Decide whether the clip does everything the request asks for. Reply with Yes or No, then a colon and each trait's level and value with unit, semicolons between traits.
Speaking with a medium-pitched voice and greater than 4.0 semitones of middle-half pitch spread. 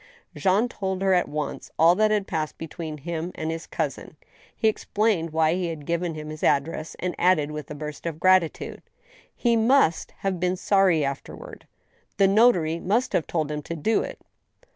No: medium, 170 Hz; average, 3.7 semitones